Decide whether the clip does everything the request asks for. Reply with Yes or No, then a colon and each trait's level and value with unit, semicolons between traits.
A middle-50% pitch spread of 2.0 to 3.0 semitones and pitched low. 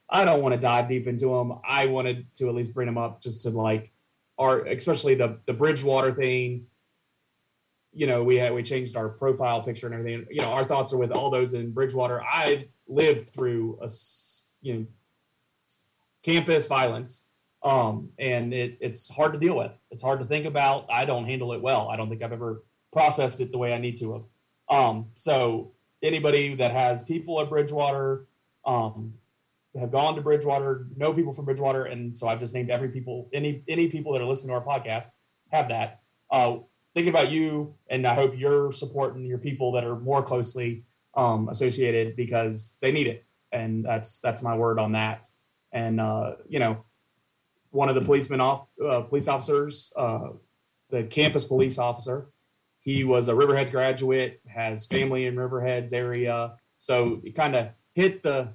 Yes: average, 2.7 semitones; low, 125 Hz